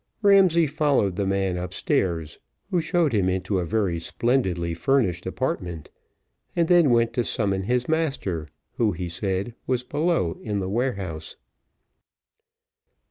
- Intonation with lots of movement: Yes, wide, 7.0 semitones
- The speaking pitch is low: Yes, low, 100 Hz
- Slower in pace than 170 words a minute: Yes, slow, 135 wpm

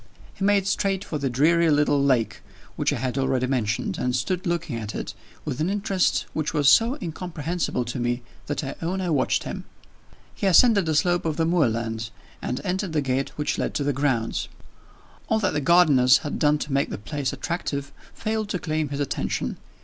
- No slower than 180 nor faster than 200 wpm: Yes, average, 195 wpm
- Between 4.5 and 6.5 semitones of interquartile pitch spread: Yes, average, 5.1 semitones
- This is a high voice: No, medium, 150 Hz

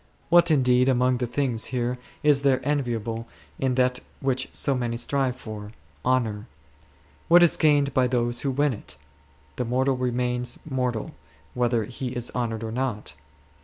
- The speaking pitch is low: Yes, low, 125 Hz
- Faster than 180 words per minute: No, average, 160 wpm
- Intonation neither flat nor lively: No, narrow, 2.0 semitones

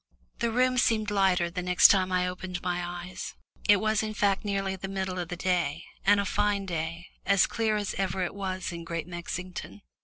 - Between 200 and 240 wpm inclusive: Yes, fast, 205 wpm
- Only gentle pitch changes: Yes, narrow, 2.2 semitones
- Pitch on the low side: No, medium, 185 Hz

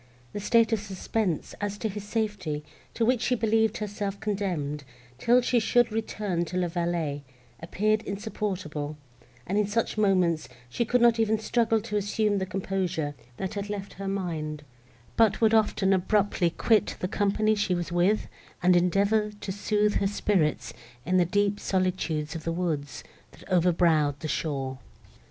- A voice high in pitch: Yes, high, 195 Hz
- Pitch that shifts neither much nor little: Yes, average, 3.7 semitones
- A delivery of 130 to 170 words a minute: Yes, average, 160 wpm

